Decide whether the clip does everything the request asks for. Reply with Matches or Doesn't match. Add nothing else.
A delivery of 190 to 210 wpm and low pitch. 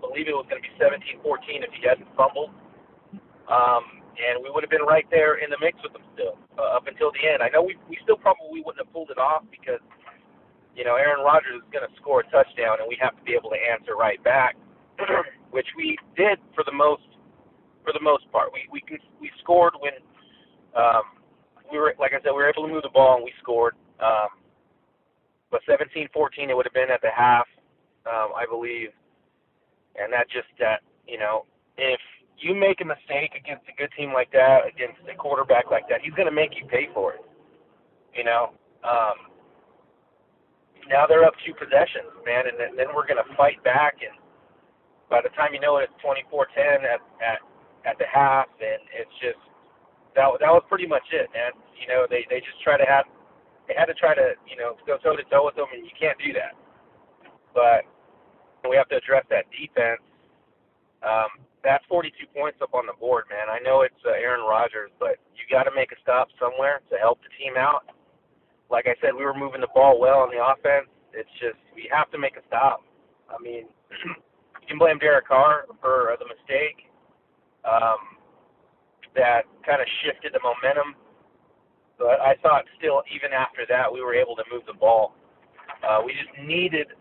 Doesn't match